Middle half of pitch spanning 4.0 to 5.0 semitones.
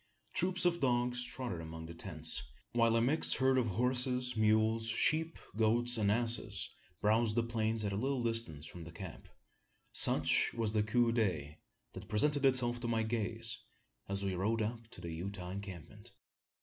No: average, 3.5 semitones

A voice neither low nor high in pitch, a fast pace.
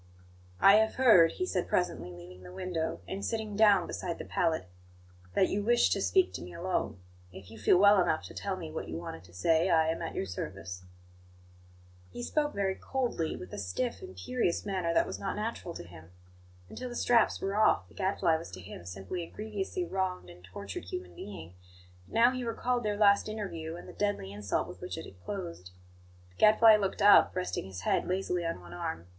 Yes: medium, 180 Hz; fast, 210 wpm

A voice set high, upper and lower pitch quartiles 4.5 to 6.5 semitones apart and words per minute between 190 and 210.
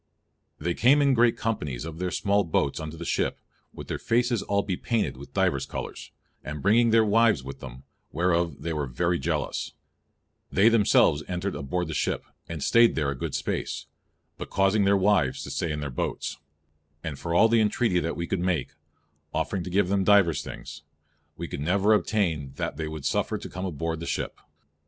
No: very low, 90 Hz; average, 4.8 semitones; average, 195 wpm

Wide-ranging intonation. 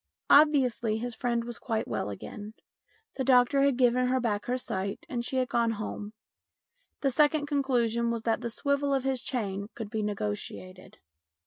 No: average, 3.3 semitones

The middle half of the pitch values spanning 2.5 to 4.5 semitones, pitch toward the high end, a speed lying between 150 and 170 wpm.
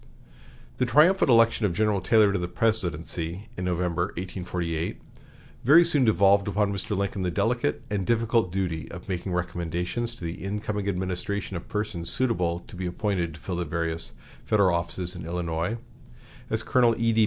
No: average, 3.8 semitones; very low, 95 Hz; average, 165 wpm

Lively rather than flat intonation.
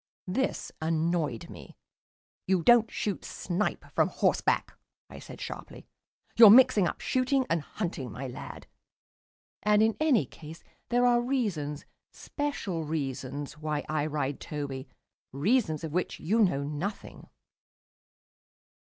Yes: wide, 7.1 semitones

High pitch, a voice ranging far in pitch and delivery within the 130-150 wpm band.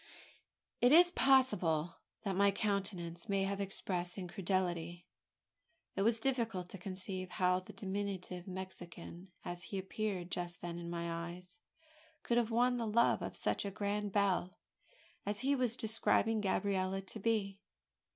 No: high, 195 Hz; average, 3.1 semitones; average, 145 wpm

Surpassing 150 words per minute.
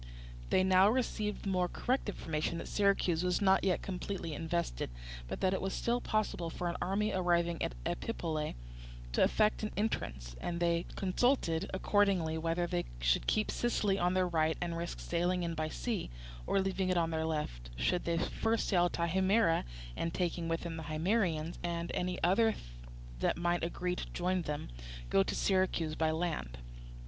Yes: average, 175 wpm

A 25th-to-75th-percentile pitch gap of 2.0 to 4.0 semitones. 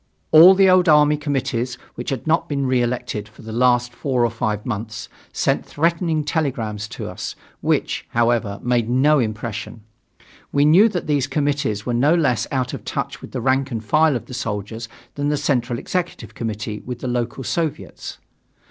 No: average, 4.4 semitones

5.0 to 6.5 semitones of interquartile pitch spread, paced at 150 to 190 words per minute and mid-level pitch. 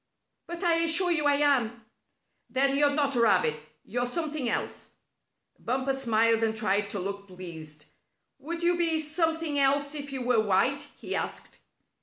No: wide, 5.6 semitones; average, 160 wpm; very high, 270 Hz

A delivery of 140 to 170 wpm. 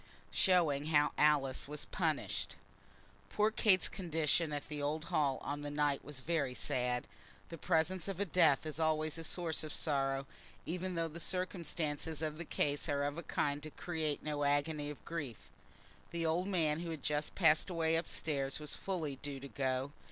No: average, 180 wpm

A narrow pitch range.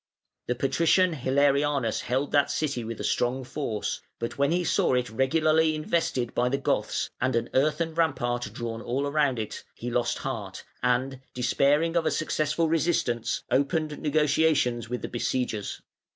No: average, 4.1 semitones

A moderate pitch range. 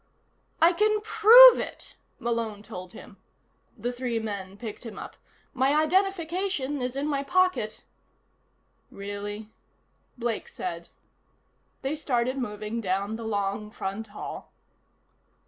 No: wide, 6.5 semitones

